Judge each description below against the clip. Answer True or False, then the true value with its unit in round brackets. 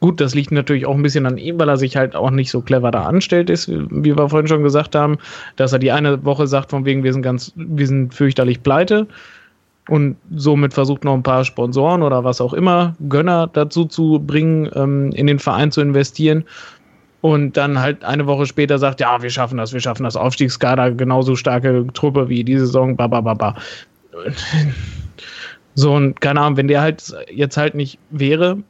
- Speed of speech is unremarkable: False (200 wpm)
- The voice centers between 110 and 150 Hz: True (140 Hz)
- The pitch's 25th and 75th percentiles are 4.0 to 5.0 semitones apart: False (2.5 semitones)